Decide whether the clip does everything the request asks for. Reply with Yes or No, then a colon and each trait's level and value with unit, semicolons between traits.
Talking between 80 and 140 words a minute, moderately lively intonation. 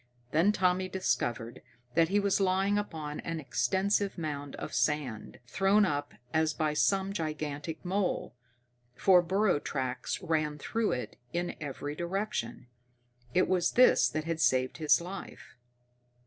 Yes: slow, 135 wpm; average, 4.5 semitones